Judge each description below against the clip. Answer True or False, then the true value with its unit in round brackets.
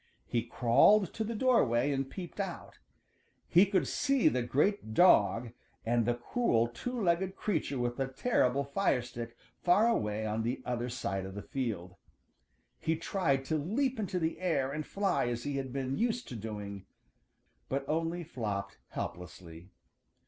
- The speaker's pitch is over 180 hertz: False (135 Hz)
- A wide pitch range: True (7.8 semitones)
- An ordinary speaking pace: True (160 wpm)